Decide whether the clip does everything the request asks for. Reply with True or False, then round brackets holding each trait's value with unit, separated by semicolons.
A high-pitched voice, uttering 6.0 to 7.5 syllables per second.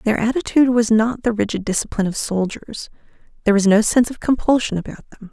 True (220 Hz; 6.5 syllables/s)